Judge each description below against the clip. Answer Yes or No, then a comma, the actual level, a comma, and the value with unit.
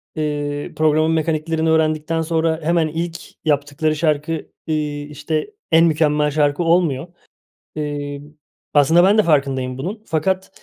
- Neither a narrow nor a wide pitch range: No, narrow, 1.9 semitones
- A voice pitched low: No, medium, 155 Hz